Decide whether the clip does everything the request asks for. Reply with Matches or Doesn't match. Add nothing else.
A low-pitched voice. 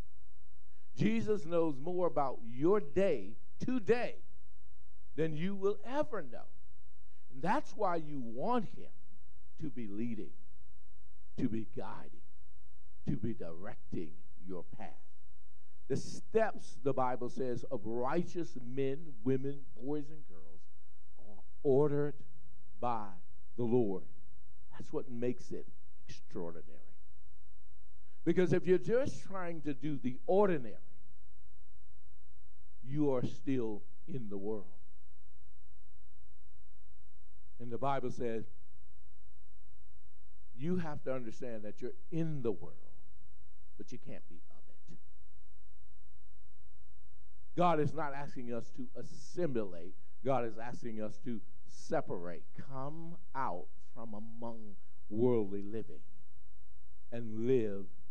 Matches